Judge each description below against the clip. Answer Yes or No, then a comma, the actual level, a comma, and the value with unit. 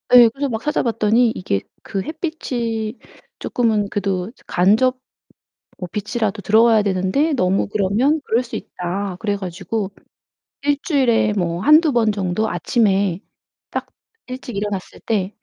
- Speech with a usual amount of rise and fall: Yes, average, 4.0 semitones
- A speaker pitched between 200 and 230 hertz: Yes, high, 215 Hz